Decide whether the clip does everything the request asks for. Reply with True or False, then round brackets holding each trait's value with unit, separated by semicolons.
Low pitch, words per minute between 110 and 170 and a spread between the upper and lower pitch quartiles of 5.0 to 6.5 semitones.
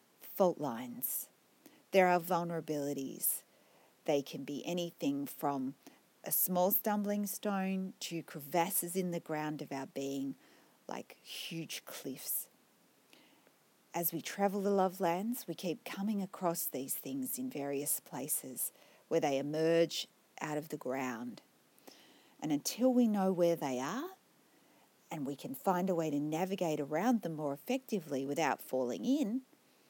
False (170 Hz; 140 wpm; 5.4 semitones)